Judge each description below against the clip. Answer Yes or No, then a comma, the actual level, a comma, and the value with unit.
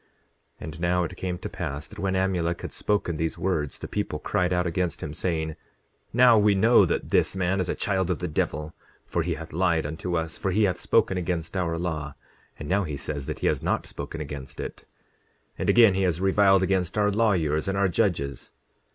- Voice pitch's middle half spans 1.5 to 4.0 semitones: Yes, average, 3.2 semitones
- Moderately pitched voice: No, very low, 90 Hz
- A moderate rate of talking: No, fast, 220 wpm